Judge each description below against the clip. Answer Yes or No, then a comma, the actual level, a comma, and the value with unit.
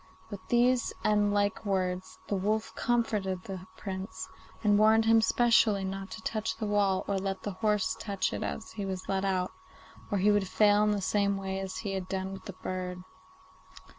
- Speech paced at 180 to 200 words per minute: Yes, average, 195 wpm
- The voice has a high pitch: Yes, high, 200 Hz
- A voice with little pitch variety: Yes, narrow, 1.9 semitones